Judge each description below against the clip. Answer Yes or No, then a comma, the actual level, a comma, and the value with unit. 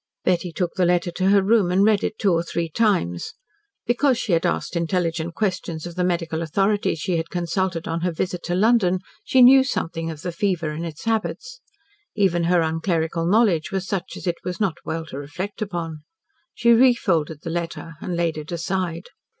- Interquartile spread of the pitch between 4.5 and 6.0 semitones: No, average, 3.1 semitones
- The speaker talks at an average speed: Yes, average, 195 wpm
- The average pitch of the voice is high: No, medium, 175 Hz